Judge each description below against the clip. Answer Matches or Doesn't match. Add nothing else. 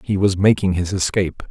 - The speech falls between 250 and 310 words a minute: Doesn't match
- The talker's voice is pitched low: Matches